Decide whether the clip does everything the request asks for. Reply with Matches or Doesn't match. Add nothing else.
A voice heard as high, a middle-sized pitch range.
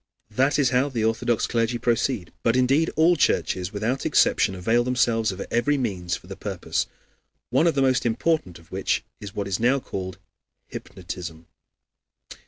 Doesn't match